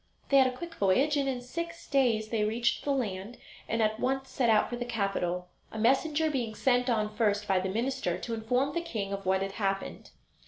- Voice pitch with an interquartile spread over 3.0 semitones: Yes, average, 4.3 semitones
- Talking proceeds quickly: Yes, fast, 220 wpm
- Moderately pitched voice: No, high, 235 Hz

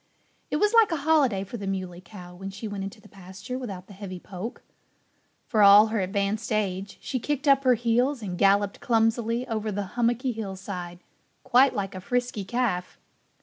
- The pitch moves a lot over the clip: No, average, 4.1 semitones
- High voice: Yes, high, 210 Hz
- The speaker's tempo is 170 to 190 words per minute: Yes, average, 185 wpm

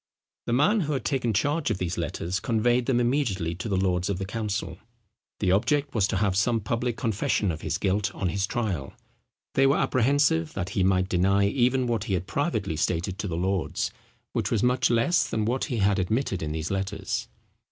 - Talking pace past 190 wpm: Yes, fast, 205 wpm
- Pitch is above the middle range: No, low, 105 Hz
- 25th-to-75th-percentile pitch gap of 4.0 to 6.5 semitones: Yes, average, 4.6 semitones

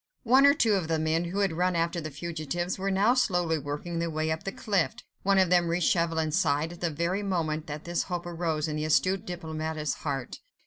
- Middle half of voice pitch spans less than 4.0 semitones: Yes, average, 2.7 semitones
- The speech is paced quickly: Yes, fast, 225 wpm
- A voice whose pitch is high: No, medium, 170 Hz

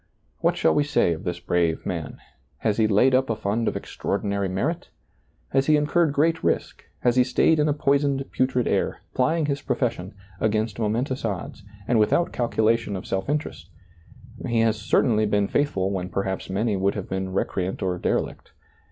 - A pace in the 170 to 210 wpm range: Yes, average, 180 wpm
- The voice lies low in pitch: Yes, low, 110 Hz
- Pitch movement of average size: No, wide, 5.7 semitones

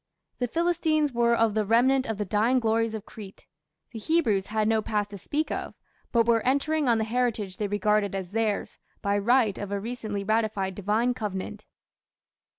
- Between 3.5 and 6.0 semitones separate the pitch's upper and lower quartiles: No, average, 3.0 semitones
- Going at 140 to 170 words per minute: No, average, 180 wpm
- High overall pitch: Yes, high, 220 Hz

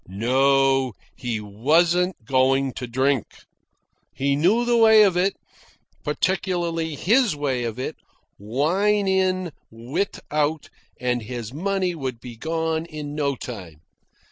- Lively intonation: Yes, wide, 6.1 semitones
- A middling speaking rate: No, slow, 125 wpm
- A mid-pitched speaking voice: Yes, medium, 145 Hz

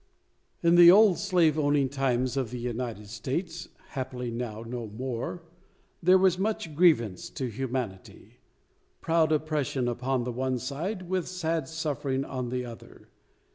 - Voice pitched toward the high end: No, low, 135 Hz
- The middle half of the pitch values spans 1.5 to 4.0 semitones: No, average, 5.2 semitones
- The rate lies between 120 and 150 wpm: Yes, average, 140 wpm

